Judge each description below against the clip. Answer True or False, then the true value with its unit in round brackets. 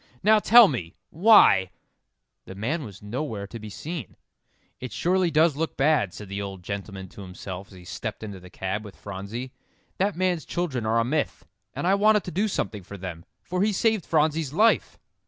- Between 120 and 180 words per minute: False (195 wpm)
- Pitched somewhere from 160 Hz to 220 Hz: False (120 Hz)